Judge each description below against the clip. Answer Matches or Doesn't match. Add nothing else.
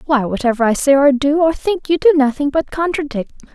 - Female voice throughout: Matches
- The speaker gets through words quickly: Matches